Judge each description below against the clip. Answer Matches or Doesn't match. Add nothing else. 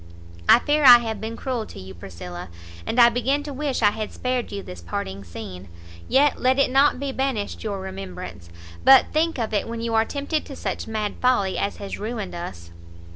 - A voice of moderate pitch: Doesn't match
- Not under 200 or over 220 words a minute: Matches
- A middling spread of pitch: Doesn't match